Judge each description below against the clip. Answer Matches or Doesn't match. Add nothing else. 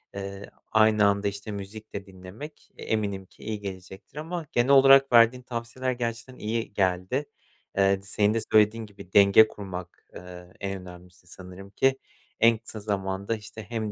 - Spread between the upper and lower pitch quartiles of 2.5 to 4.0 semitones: Matches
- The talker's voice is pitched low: Matches